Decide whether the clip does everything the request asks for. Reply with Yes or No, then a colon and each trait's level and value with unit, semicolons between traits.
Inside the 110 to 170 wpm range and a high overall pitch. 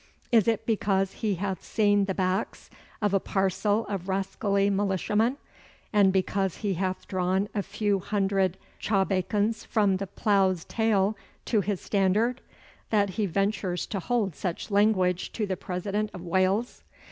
Yes: average, 145 wpm; high, 195 Hz